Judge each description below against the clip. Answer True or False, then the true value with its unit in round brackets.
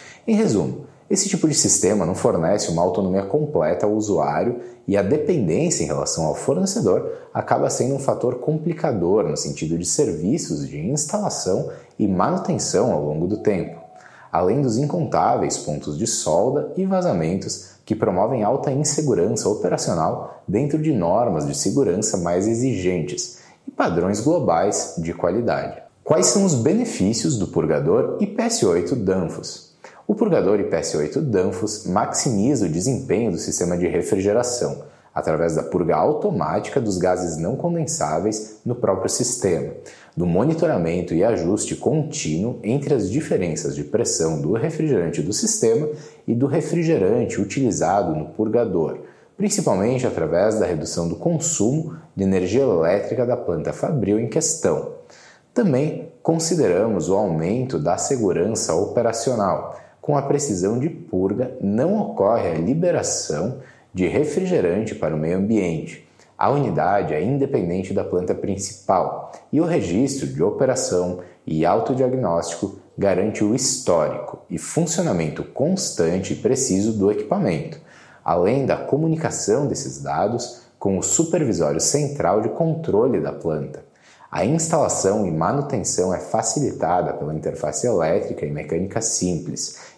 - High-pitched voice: False (115 Hz)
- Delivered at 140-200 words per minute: False (130 wpm)